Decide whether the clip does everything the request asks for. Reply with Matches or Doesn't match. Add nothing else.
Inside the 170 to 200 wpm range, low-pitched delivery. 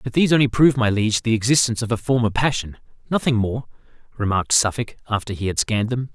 Matches